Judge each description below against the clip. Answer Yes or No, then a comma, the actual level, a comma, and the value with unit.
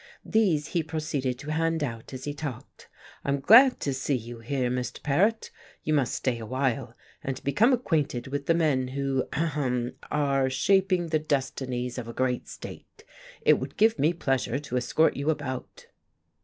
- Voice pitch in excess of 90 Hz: Yes, medium, 140 Hz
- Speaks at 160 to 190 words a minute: Yes, average, 170 wpm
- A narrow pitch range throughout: No, average, 3.7 semitones